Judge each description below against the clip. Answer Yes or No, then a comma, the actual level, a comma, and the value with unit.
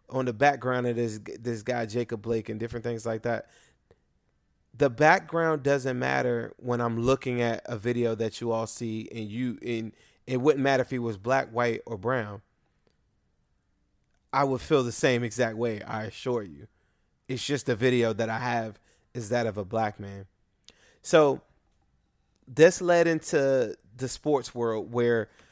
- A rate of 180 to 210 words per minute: No, average, 170 wpm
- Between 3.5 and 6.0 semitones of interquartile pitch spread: No, narrow, 2.5 semitones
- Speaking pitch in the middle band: No, low, 120 Hz